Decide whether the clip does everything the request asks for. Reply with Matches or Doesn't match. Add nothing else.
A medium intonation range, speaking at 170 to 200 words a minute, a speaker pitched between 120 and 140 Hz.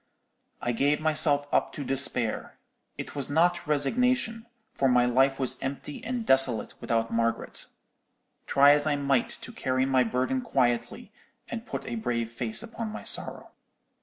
Doesn't match